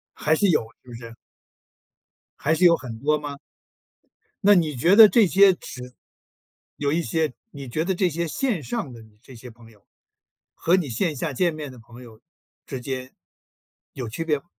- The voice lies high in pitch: No, medium, 145 Hz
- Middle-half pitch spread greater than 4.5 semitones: Yes, wide, 5.5 semitones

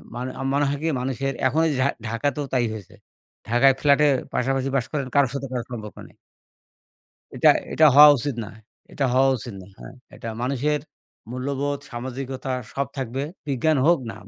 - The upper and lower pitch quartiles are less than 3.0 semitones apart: Yes, narrow, 2.4 semitones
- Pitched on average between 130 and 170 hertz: Yes, low, 135 Hz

